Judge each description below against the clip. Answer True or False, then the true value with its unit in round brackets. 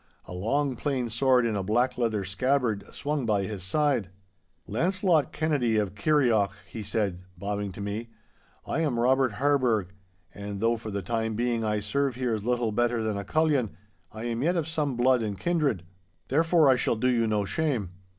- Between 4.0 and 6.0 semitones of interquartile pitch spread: True (4.8 semitones)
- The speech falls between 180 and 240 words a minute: True (185 wpm)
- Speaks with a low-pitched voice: True (115 Hz)